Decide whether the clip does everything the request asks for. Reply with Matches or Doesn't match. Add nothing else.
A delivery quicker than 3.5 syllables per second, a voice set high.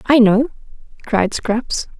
Doesn't match